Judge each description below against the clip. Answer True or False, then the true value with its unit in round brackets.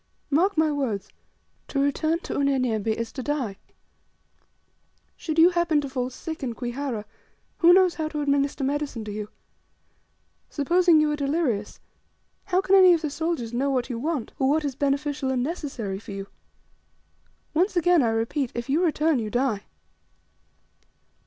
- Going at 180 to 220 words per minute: False (160 wpm)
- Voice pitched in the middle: False (280 Hz)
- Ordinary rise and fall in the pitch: True (4.7 semitones)